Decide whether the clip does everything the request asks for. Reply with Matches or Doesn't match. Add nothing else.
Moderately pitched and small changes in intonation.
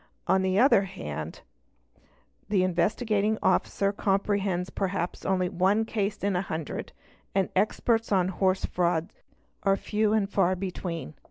Doesn't match